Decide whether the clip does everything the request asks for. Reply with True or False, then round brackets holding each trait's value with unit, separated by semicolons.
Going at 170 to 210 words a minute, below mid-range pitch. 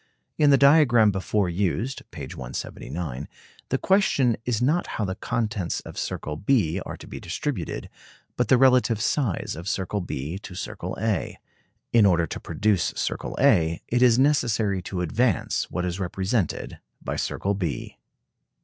False (155 wpm; 105 Hz)